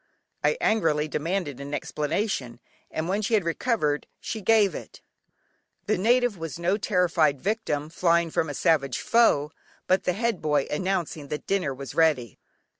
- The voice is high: No, medium, 165 Hz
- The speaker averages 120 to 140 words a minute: No, average, 155 wpm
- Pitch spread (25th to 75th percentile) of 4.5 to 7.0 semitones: Yes, average, 5.2 semitones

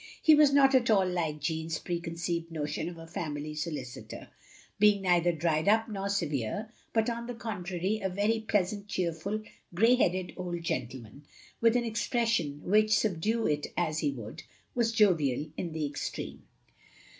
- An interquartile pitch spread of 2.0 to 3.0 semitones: No, wide, 5.4 semitones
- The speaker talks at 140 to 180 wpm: Yes, average, 155 wpm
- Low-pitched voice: No, medium, 180 Hz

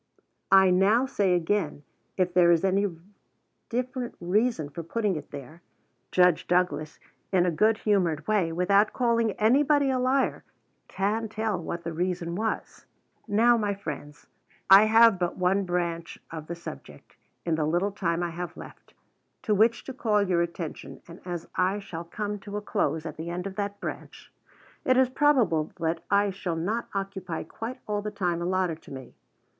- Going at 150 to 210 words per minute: Yes, average, 170 wpm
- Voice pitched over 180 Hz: Yes, high, 190 Hz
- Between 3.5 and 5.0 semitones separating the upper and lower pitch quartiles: Yes, average, 3.9 semitones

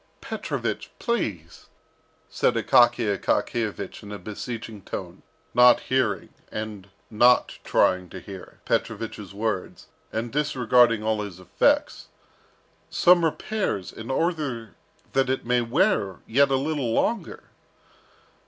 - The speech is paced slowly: Yes, slow, 115 wpm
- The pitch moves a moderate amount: Yes, average, 4.4 semitones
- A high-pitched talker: No, low, 115 Hz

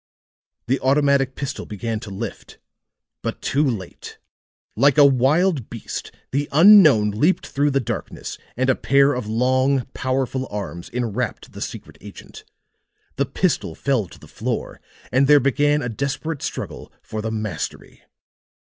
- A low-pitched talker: Yes, low, 130 Hz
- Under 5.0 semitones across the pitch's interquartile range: Yes, average, 3.7 semitones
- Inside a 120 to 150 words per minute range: Yes, average, 145 wpm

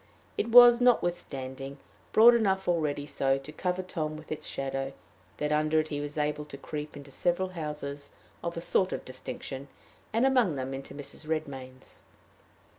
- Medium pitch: Yes, medium, 150 Hz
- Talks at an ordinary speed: Yes, average, 165 wpm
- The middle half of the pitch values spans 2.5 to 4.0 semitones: No, average, 4.4 semitones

